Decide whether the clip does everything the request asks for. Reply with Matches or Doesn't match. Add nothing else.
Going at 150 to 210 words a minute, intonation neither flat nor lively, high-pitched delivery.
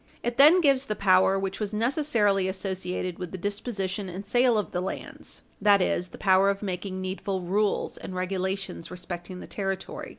Doesn't match